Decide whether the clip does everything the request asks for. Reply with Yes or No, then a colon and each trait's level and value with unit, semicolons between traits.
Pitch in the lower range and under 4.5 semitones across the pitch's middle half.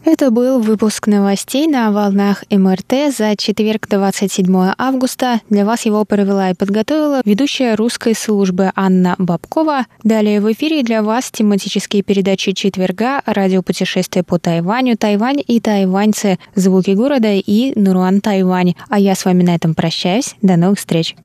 No: high, 205 Hz; average, 3.2 semitones